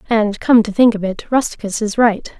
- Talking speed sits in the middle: No, fast, 225 wpm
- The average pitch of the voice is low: No, high, 220 Hz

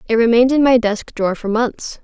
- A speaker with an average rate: No, fast, 235 wpm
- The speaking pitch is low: No, high, 235 Hz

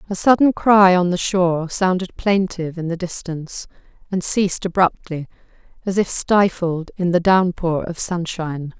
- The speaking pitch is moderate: Yes, medium, 180 Hz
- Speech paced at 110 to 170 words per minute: Yes, average, 150 wpm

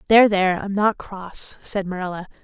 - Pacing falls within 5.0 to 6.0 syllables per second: Yes, 5.5 syllables/s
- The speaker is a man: No, female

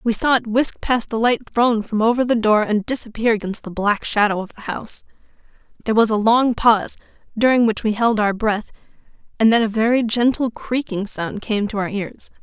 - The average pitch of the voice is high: Yes, high, 220 Hz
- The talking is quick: Yes, fast, 210 wpm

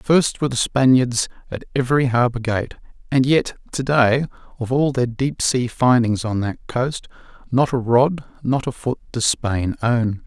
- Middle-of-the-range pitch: No, low, 125 Hz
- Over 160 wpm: Yes, average, 170 wpm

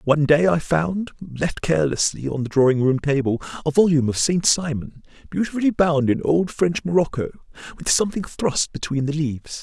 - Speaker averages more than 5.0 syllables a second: Yes, 5.5 syllables/s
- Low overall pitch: No, medium, 155 Hz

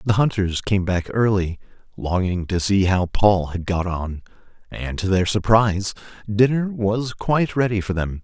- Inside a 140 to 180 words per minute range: Yes, average, 170 wpm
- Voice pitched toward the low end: Yes, low, 100 Hz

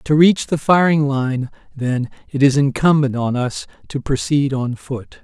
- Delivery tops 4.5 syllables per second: No, 4.2 syllables/s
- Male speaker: Yes, male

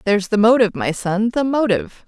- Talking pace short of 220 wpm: Yes, average, 200 wpm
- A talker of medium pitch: No, high, 220 Hz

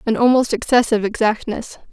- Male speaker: No, female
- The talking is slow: Yes, slow, 125 wpm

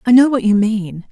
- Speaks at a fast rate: Yes, fast, 270 wpm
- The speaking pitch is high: Yes, high, 220 Hz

